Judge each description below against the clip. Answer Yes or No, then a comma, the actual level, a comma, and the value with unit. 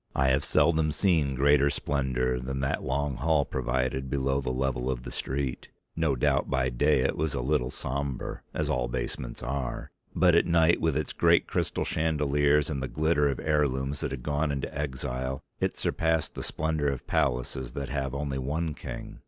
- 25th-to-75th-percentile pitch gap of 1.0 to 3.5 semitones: Yes, narrow, 2.4 semitones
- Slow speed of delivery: No, average, 185 wpm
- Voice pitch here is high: No, very low, 70 Hz